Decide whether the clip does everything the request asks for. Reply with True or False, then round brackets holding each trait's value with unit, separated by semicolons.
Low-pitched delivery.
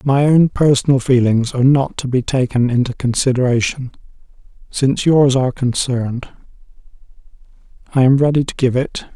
True (130 Hz)